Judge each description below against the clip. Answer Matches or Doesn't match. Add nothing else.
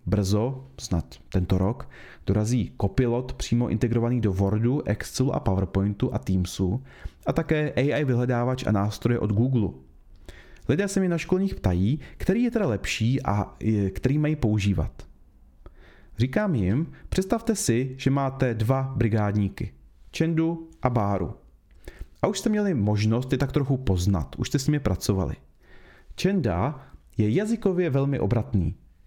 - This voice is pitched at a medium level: Doesn't match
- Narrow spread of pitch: Doesn't match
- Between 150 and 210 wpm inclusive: Doesn't match